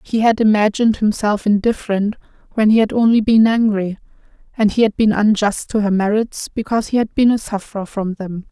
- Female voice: Yes, female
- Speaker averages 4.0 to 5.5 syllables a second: No, 5.7 syllables/s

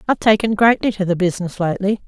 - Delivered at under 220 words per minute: Yes, average, 200 wpm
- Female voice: Yes, female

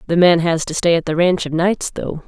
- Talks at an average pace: No, fast, 290 wpm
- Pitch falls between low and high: Yes, medium, 170 Hz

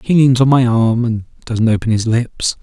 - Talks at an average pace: No, fast, 230 wpm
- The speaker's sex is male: Yes, male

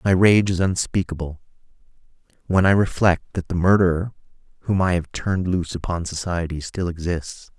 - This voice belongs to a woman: No, male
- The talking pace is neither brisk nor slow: Yes, average, 150 wpm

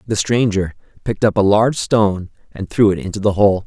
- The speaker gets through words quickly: Yes, fast, 215 wpm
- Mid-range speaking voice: No, low, 105 Hz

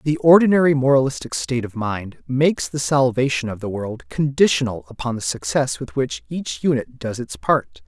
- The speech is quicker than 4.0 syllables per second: Yes, 5.1 syllables/s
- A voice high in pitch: No, low, 130 Hz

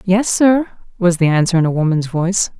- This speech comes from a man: No, female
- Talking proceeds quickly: Yes, fast, 210 wpm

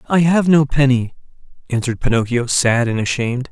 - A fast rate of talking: No, average, 155 wpm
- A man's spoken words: Yes, male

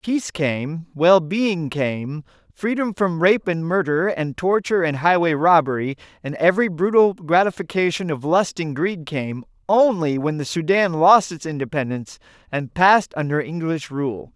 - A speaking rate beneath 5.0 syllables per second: Yes, 4.6 syllables/s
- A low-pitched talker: No, medium, 165 Hz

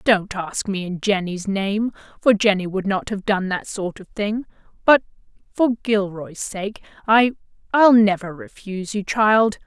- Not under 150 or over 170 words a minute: Yes, average, 155 wpm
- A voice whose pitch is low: No, high, 205 Hz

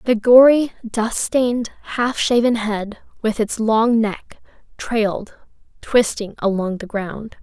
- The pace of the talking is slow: Yes, slow, 130 wpm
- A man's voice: No, female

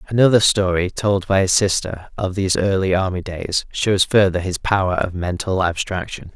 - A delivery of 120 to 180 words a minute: Yes, average, 170 wpm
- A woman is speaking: No, male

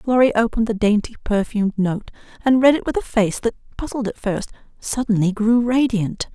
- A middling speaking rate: Yes, average, 180 wpm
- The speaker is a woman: Yes, female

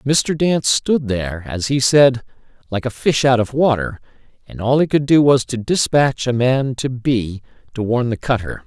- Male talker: Yes, male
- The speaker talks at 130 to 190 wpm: No, average, 200 wpm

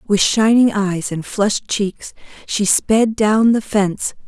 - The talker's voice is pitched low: No, high, 210 Hz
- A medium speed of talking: Yes, average, 155 wpm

